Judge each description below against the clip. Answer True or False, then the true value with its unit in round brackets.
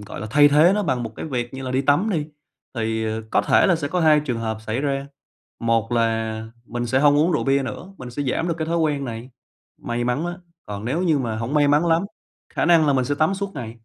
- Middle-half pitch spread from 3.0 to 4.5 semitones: False (5.1 semitones)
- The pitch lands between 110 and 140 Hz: True (135 Hz)